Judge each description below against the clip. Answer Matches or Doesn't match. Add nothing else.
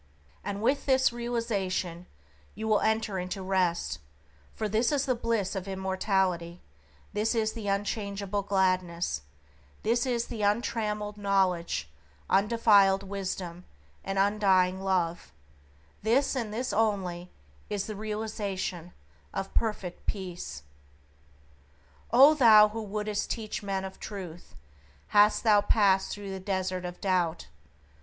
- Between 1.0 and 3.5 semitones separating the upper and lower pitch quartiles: Matches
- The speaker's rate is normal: Doesn't match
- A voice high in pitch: Matches